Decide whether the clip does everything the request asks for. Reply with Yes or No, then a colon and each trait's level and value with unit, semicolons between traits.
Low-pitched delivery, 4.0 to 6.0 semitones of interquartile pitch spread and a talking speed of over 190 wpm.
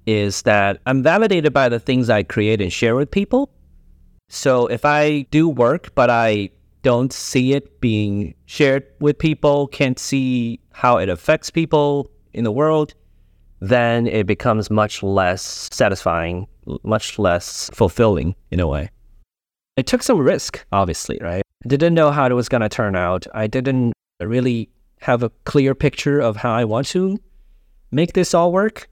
No: low, 120 Hz; wide, 5.6 semitones; average, 165 wpm